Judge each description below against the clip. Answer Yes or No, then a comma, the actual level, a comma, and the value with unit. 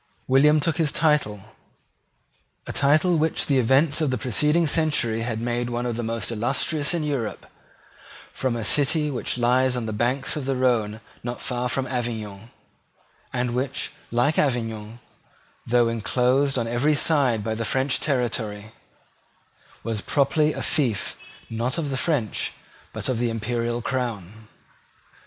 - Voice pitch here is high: No, low, 125 Hz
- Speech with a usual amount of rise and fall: Yes, average, 3.7 semitones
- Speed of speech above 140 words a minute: Yes, average, 150 wpm